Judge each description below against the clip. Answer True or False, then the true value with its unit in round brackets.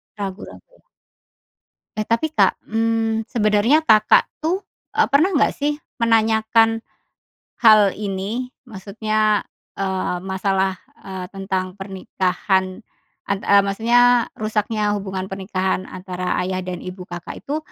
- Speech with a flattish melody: False (3.1 semitones)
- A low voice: False (210 Hz)